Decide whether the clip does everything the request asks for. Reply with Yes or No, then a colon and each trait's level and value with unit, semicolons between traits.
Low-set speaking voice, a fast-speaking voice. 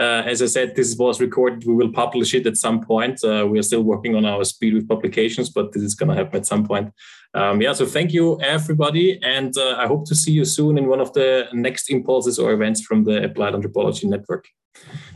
Yes: low, 120 Hz; fast, 240 wpm